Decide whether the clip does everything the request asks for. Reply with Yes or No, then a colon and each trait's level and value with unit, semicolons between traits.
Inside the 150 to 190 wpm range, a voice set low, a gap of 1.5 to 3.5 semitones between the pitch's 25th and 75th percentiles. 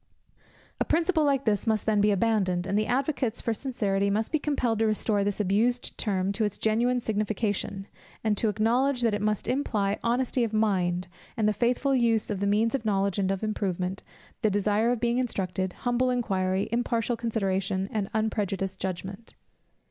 No: average, 180 wpm; high, 215 Hz; average, 3.2 semitones